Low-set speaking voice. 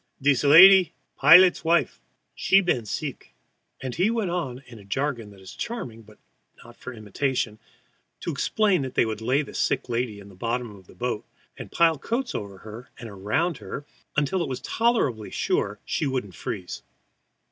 Yes: low, 130 Hz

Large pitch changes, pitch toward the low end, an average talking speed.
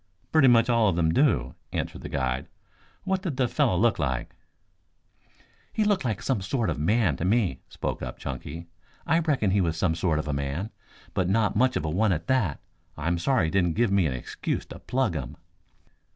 No: wide, 7.3 semitones; very low, 95 Hz; fast, 210 wpm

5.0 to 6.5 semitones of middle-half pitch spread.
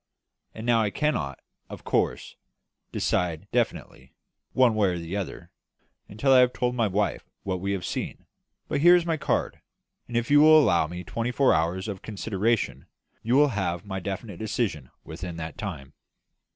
Yes: wide, 5.6 semitones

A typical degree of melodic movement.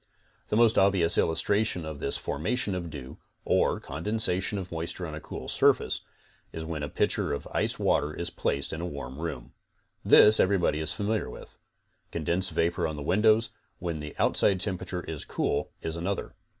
Yes: average, 4.1 semitones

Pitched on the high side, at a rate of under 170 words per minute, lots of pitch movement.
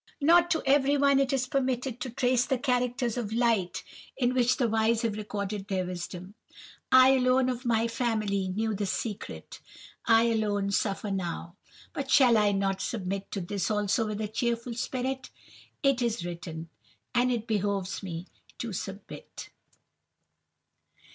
No: high, 225 Hz; average, 150 wpm; average, 4.2 semitones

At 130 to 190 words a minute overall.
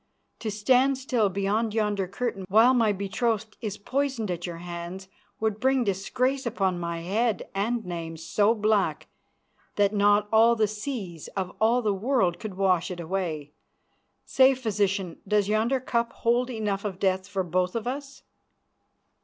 Yes: average, 155 wpm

